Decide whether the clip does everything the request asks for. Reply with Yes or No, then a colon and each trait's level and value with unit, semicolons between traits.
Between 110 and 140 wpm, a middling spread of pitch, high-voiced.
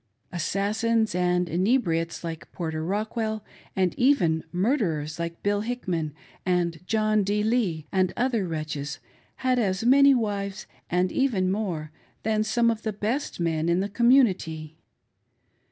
Yes: slow, 135 wpm; average, 4.9 semitones; high, 195 Hz